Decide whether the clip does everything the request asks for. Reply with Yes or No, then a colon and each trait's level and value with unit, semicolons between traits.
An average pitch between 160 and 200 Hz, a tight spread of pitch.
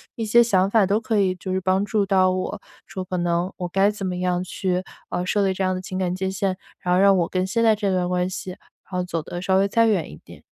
Yes: medium, 185 Hz; narrow, 1.7 semitones